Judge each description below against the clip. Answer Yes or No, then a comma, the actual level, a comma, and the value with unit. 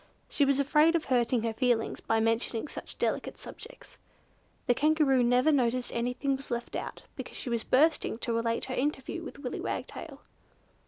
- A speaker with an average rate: Yes, average, 175 wpm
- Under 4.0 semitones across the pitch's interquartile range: Yes, average, 3.2 semitones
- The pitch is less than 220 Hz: No, very high, 255 Hz